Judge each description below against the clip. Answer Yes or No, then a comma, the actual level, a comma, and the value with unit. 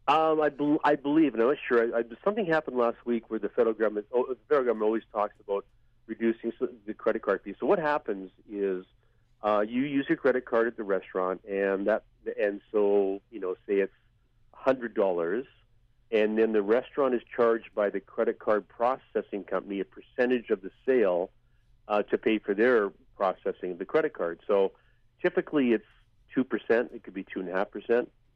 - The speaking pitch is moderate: No, low, 115 Hz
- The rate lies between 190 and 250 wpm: Yes, fast, 205 wpm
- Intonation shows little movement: No, average, 3.2 semitones